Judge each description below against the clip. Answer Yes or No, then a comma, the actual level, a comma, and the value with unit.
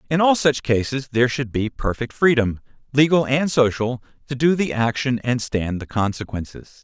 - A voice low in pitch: Yes, low, 125 Hz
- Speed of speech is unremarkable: Yes, average, 175 wpm